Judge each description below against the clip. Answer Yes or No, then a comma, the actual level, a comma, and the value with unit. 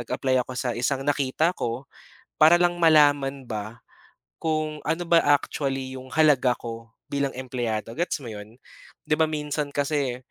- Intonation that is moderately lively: Yes, average, 3.6 semitones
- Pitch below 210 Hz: Yes, low, 135 Hz